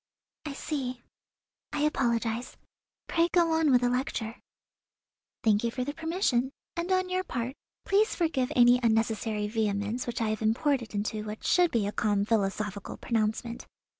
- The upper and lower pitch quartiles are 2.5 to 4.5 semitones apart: No, average, 5.2 semitones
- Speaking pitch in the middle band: No, high, 240 Hz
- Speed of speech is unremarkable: Yes, average, 155 wpm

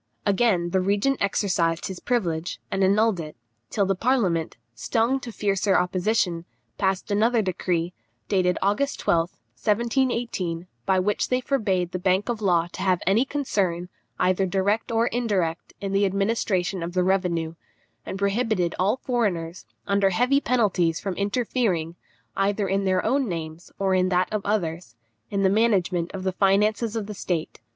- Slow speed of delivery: No, average, 160 wpm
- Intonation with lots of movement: No, average, 3.3 semitones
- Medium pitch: No, high, 195 Hz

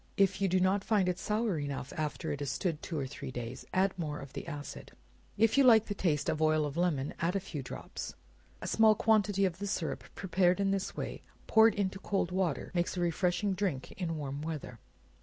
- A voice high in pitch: No, medium, 180 Hz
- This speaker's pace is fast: Yes, fast, 215 wpm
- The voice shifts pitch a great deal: No, average, 4.7 semitones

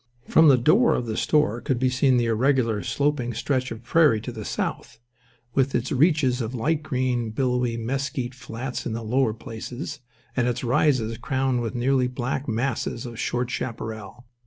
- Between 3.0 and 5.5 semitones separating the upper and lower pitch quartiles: No, narrow, 2.6 semitones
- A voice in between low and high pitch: No, low, 125 Hz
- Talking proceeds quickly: No, average, 175 wpm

